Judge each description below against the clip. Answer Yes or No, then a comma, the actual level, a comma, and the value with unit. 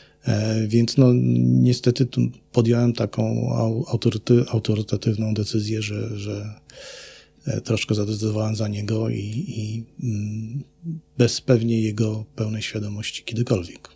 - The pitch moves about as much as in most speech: No, narrow, 1.9 semitones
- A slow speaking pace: Yes, slow, 100 wpm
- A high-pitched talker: No, low, 110 Hz